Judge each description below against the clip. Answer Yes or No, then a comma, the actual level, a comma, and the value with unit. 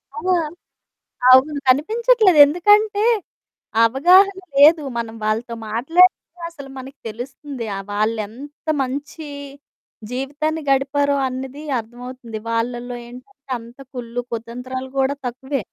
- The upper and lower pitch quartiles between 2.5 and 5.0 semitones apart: Yes, average, 3.9 semitones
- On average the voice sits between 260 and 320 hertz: Yes, very high, 265 Hz